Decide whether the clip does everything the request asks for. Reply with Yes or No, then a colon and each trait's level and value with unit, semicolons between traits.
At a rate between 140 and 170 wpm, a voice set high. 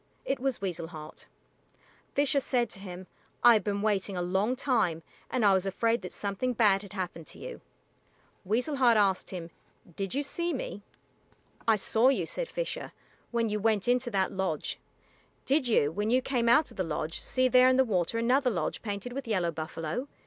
No: average, 190 wpm; high, 215 Hz